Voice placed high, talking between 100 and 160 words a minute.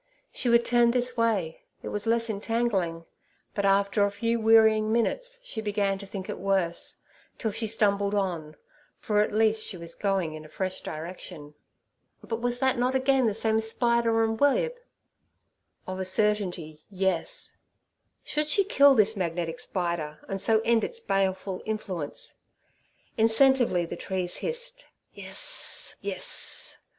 Yes: high, 215 Hz; average, 150 wpm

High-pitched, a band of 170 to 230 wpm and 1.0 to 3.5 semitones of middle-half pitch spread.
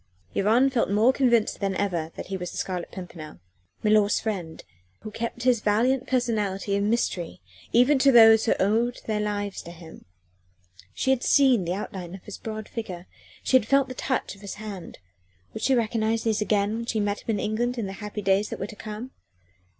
Yes: high, 215 Hz; average, 200 wpm; average, 3.2 semitones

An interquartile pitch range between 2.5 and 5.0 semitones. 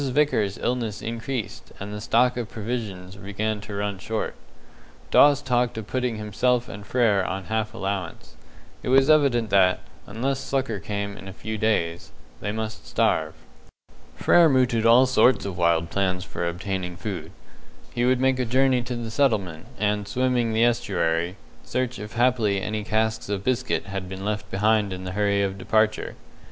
Yes: average, 3.9 semitones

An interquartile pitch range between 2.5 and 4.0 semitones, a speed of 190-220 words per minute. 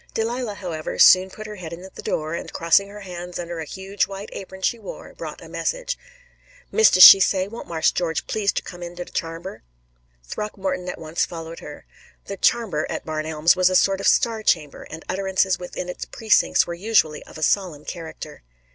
Yes: average, 3.1 semitones; average, 200 wpm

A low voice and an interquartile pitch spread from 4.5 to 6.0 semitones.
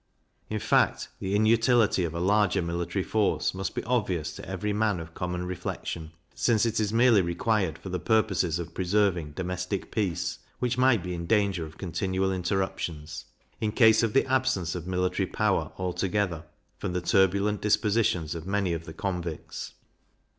No: very low, 95 Hz; average, 3.5 semitones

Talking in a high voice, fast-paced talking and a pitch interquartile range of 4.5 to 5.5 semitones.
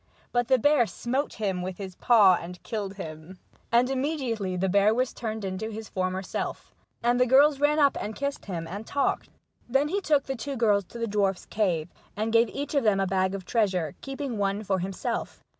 Yes: high, 215 Hz; fast, 210 wpm; average, 5.2 semitones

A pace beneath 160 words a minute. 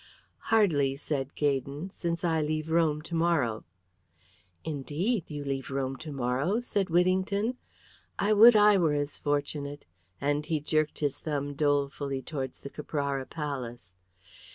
Yes: slow, 135 wpm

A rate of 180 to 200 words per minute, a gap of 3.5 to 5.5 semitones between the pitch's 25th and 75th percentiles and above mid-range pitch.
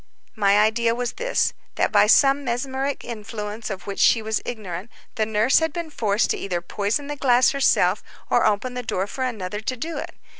Yes: average, 190 wpm; average, 4.0 semitones; high, 230 Hz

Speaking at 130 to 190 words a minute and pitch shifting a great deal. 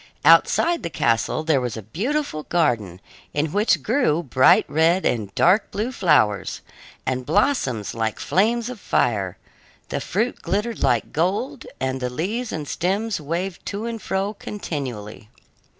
Yes: average, 145 wpm; wide, 9.0 semitones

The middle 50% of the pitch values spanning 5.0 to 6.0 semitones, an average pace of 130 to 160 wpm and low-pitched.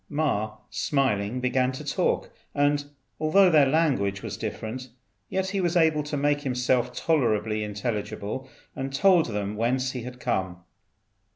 Yes: average, 5.3 semitones; average, 145 wpm; low, 130 Hz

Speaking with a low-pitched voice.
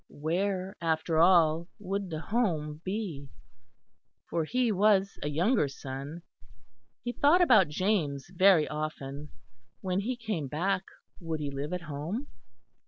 No: medium, 175 Hz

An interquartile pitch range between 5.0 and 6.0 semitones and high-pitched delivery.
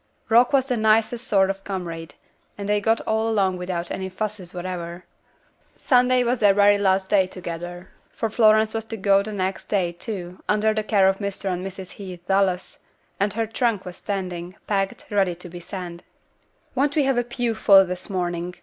No: average, 3.1 semitones; high, 195 Hz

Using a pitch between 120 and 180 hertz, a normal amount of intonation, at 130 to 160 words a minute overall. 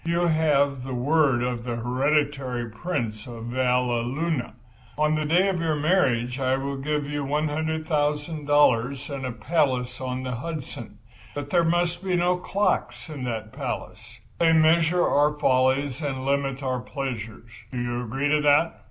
Yes: medium, 140 Hz; average, 3.8 semitones; average, 150 wpm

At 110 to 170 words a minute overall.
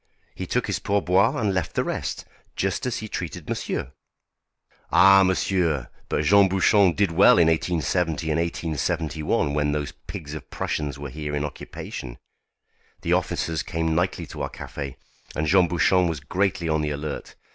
Yes: average, 165 wpm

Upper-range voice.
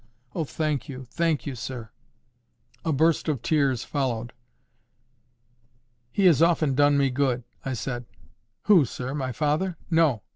No: medium, 140 Hz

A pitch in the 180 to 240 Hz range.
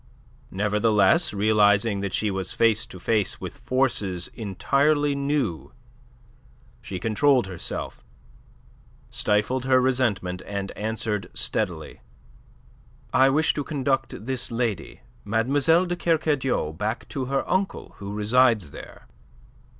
No: low, 115 Hz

